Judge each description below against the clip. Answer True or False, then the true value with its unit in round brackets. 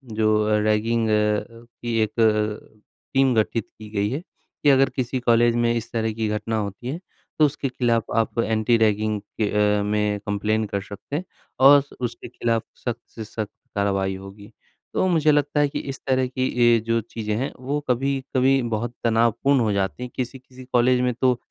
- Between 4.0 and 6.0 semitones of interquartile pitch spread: False (3.3 semitones)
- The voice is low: True (115 Hz)